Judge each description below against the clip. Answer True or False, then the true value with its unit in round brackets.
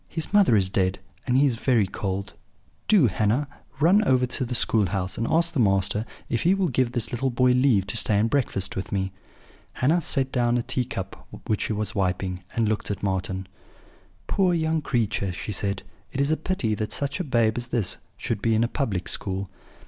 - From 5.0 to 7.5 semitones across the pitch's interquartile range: True (5.4 semitones)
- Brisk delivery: True (210 wpm)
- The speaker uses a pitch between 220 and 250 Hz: False (115 Hz)